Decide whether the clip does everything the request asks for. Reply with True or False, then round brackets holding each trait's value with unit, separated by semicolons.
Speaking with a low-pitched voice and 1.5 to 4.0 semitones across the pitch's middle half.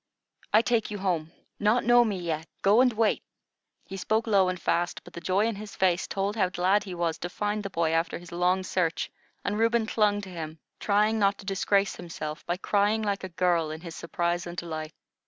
False (190 Hz; 3.4 semitones)